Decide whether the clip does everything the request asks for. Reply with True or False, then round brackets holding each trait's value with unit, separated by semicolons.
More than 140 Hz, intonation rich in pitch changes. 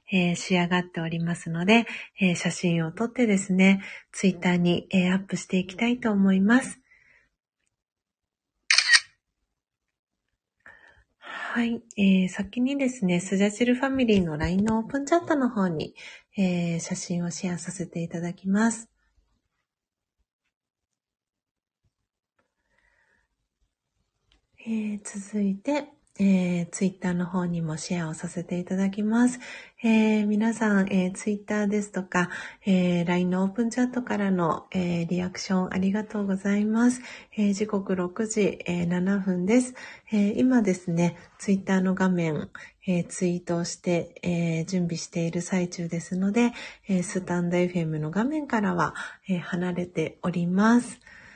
False (190 Hz; 3.6 semitones)